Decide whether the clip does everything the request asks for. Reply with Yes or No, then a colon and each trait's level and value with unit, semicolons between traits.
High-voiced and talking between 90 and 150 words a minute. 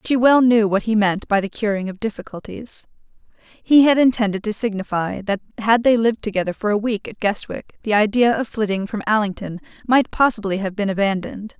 No: high, 215 Hz; average, 190 wpm